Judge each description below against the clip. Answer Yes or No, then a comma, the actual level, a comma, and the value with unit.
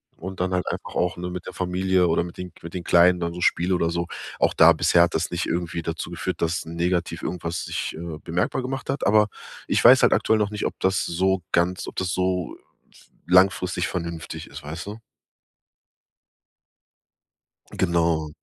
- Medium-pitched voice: No, very low, 90 Hz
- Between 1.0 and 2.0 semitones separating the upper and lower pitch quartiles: Yes, narrow, 1.6 semitones